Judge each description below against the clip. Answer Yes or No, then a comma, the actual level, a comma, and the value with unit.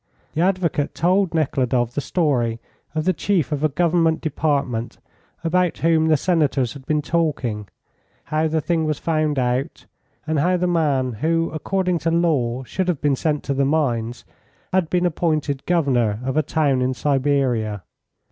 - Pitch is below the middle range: No, medium, 150 Hz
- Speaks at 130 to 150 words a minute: No, average, 165 wpm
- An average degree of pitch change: Yes, average, 3.9 semitones